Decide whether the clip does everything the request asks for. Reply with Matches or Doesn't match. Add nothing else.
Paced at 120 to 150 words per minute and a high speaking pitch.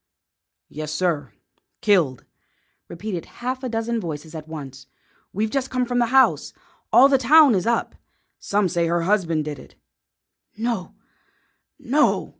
Matches